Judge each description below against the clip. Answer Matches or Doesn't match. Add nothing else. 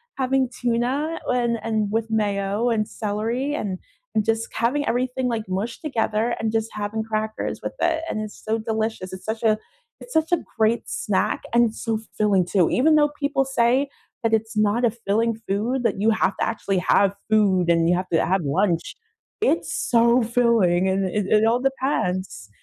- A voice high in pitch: Matches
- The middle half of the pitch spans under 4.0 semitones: Matches